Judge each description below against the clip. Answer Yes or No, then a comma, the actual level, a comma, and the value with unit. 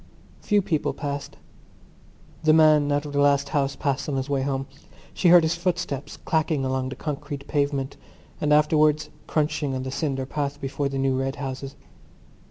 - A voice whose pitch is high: No, medium, 145 Hz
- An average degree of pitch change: No, narrow, 2.0 semitones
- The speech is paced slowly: No, average, 175 wpm